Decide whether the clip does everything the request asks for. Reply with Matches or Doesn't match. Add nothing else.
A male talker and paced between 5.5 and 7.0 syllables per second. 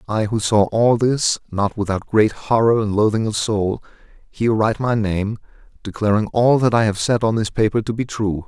Doesn't match